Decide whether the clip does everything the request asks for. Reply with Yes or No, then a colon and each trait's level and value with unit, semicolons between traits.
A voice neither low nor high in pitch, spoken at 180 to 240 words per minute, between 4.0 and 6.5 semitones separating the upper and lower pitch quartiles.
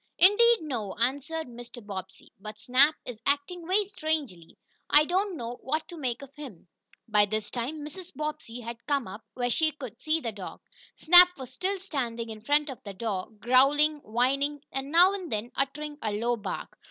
No: very high, 270 Hz; average, 185 wpm; average, 5.3 semitones